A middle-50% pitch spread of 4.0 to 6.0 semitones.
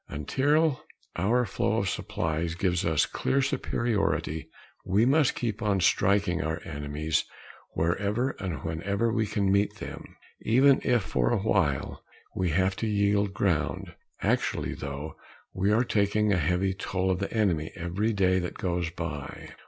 Yes: average, 4.3 semitones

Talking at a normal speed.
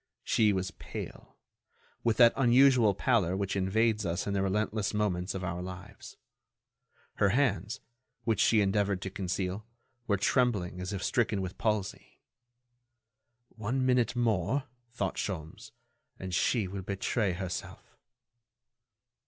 No: slow, 125 wpm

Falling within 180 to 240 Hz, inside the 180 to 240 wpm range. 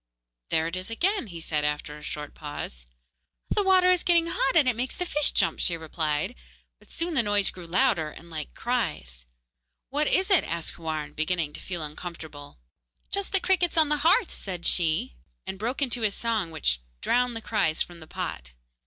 Yes: medium, 185 Hz; average, 195 wpm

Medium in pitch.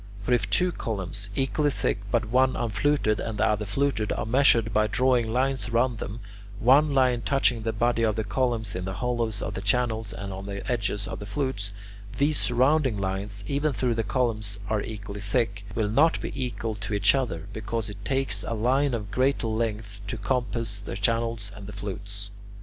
No: low, 110 Hz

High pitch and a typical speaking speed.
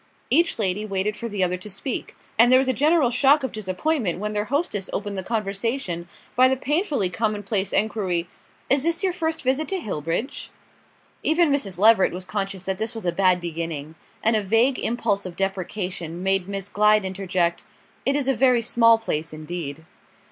Yes: high, 210 Hz; average, 185 wpm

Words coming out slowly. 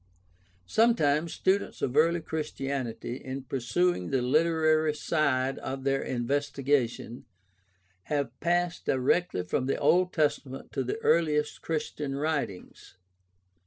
Yes: slow, 110 wpm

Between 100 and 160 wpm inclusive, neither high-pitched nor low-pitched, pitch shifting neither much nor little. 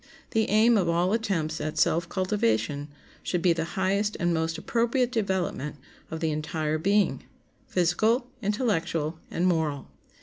Yes: slow, 135 wpm; medium, 175 Hz; average, 4.5 semitones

